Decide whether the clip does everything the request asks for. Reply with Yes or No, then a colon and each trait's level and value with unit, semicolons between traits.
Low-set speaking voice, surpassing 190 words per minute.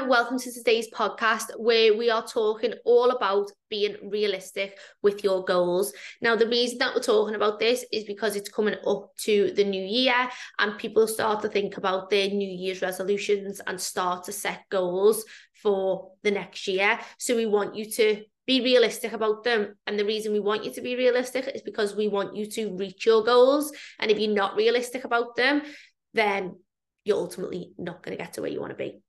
No: high, 215 Hz; average, 200 wpm